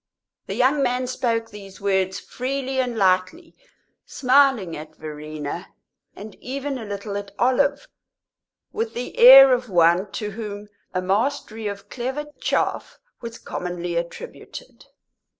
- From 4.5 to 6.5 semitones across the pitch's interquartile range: Yes, wide, 5.5 semitones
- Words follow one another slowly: Yes, slow, 130 wpm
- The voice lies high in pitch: Yes, high, 225 Hz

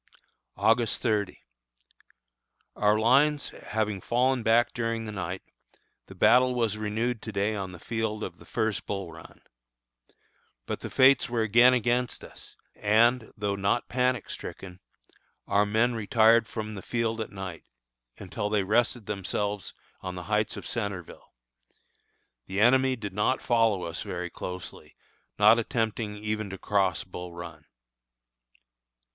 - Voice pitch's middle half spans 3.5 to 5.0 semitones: No, average, 3.0 semitones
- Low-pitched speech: Yes, low, 110 Hz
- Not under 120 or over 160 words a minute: Yes, average, 140 wpm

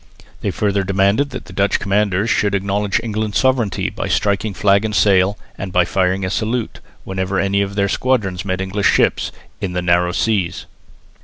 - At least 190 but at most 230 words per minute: No, average, 170 wpm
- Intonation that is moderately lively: No, narrow, 1.9 semitones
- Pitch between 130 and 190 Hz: No, low, 100 Hz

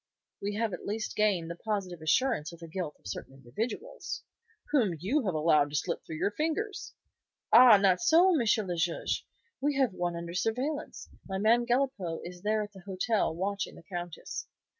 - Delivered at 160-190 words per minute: Yes, average, 180 wpm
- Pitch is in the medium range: No, high, 195 Hz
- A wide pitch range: Yes, wide, 5.8 semitones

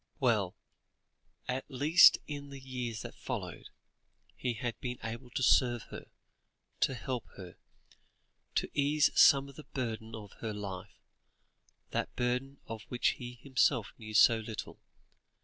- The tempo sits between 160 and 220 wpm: No, average, 140 wpm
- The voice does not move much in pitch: No, average, 3.2 semitones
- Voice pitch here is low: Yes, low, 125 Hz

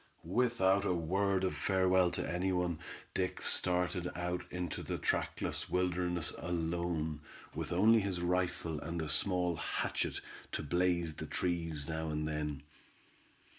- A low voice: Yes, very low, 90 Hz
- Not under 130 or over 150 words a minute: Yes, slow, 135 wpm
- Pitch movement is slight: Yes, narrow, 2.1 semitones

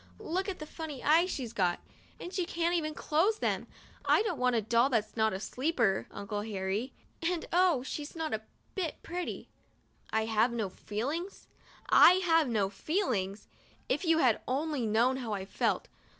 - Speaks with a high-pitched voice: Yes, very high, 260 Hz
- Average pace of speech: Yes, average, 165 wpm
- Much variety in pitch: Yes, wide, 7.2 semitones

